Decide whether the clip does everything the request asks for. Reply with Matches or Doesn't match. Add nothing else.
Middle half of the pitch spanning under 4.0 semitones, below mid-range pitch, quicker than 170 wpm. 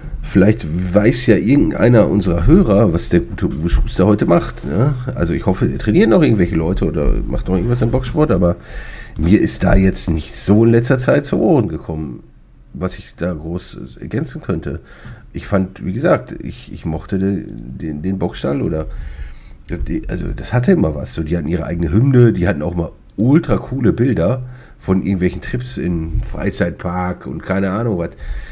Doesn't match